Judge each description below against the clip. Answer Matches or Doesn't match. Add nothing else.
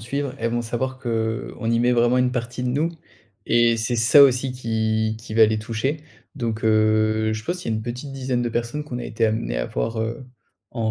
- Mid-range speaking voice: Doesn't match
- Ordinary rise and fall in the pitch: Doesn't match